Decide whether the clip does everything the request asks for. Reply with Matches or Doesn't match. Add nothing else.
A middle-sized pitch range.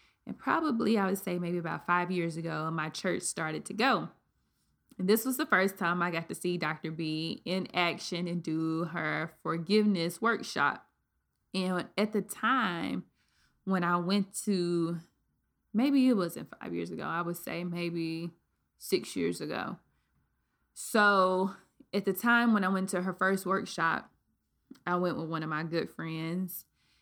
Matches